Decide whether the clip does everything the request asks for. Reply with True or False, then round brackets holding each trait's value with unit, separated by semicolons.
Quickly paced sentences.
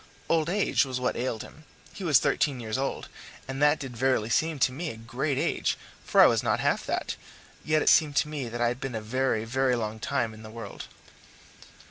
True (220 wpm)